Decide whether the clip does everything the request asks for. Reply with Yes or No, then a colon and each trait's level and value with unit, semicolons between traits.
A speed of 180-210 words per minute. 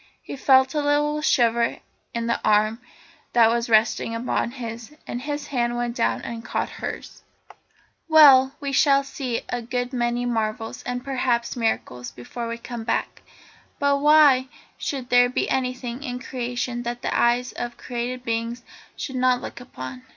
No: average, 160 wpm